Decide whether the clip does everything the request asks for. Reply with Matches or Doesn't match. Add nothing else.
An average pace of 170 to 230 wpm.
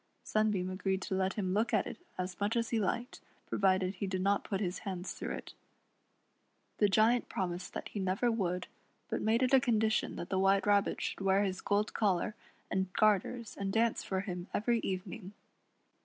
Matches